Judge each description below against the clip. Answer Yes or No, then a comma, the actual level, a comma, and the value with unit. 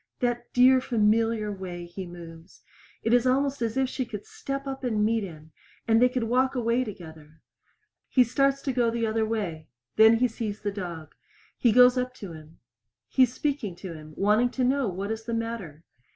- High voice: Yes, high, 225 Hz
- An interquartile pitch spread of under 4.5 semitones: No, average, 4.8 semitones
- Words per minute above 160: Yes, average, 195 wpm